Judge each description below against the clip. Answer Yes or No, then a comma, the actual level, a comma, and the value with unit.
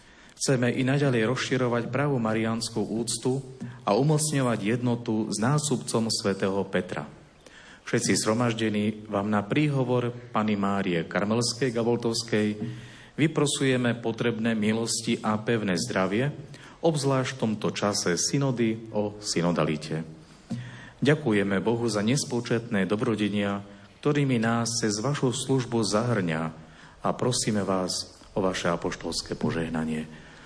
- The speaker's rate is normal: No, slow, 105 wpm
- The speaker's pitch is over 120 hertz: No, low, 115 Hz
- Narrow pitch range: No, average, 3.6 semitones